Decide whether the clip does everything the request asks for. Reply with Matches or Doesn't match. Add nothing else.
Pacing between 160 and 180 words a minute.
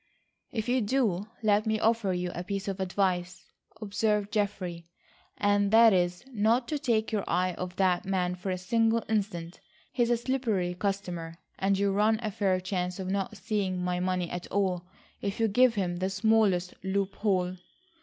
Matches